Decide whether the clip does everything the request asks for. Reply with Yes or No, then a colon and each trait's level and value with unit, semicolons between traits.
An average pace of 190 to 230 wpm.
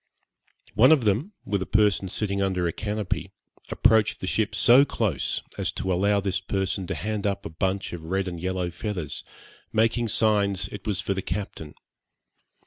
No: average, 175 wpm